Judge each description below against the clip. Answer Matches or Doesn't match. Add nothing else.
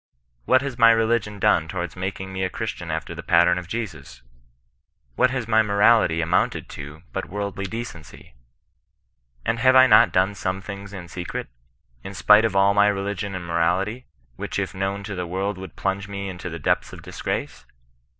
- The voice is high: Doesn't match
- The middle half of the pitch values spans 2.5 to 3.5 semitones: Matches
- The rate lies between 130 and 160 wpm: Doesn't match